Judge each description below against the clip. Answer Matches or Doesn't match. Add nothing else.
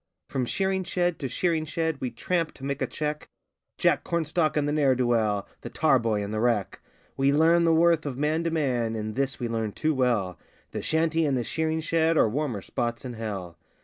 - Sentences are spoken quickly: Matches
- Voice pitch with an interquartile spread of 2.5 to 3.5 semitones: Doesn't match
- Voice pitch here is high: Doesn't match